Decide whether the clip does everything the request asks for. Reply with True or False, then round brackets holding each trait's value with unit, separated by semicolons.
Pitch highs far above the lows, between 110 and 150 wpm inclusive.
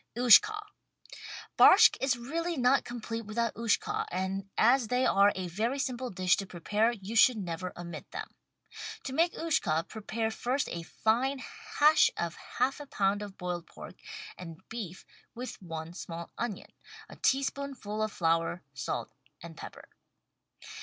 True (6.1 semitones; 145 wpm)